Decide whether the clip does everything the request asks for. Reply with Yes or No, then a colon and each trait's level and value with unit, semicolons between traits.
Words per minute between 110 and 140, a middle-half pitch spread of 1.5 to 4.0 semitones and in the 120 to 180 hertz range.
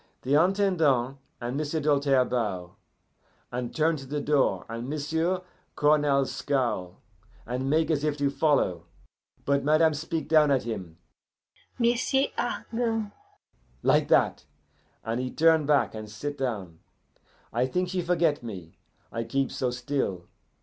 No: slow, 135 wpm; average, 4.6 semitones; medium, 140 Hz